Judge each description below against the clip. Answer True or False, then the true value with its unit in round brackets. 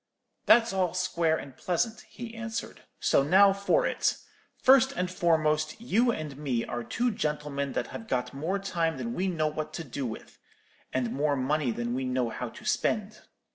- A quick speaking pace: False (180 wpm)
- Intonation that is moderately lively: False (6.2 semitones)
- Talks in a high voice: False (155 Hz)